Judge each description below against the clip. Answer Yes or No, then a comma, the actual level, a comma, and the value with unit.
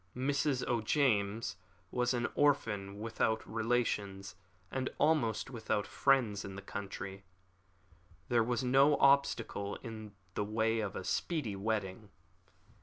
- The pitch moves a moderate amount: Yes, average, 4.1 semitones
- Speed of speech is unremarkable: No, slow, 115 wpm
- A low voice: Yes, low, 110 Hz